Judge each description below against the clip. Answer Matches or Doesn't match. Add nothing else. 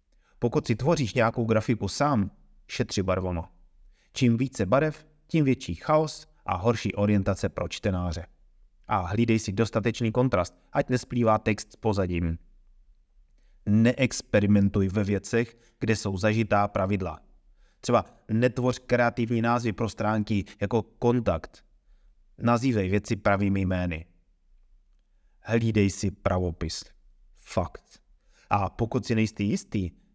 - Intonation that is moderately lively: Matches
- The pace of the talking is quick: Doesn't match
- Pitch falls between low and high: Doesn't match